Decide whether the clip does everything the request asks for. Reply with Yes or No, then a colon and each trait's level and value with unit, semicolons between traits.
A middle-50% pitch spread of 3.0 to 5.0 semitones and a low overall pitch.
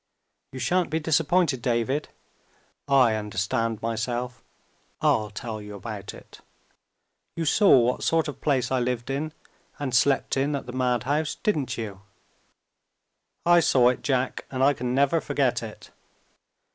Yes: average, 3.7 semitones; low, 130 Hz